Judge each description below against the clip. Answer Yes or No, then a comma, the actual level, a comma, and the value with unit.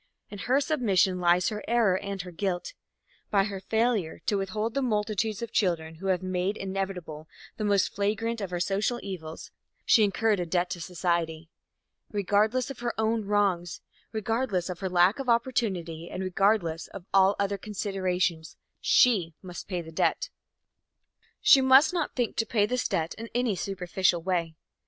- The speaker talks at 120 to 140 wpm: No, average, 165 wpm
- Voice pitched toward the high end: Yes, high, 195 Hz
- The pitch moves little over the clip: No, average, 3.7 semitones